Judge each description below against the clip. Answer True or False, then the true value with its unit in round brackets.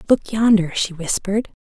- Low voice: False (200 Hz)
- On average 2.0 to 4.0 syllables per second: False (5.3 syllables/s)